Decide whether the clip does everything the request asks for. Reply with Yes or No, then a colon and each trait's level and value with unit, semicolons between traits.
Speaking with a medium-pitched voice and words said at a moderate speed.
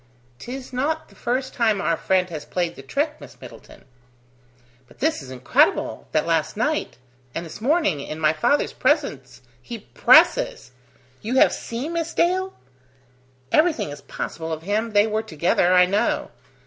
No: high, 215 Hz; average, 160 wpm